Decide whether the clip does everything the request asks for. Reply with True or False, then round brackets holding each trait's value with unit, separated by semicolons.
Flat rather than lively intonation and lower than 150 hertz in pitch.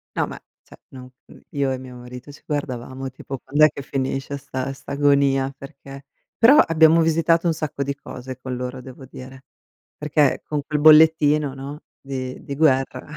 True (2.3 semitones; 140 Hz)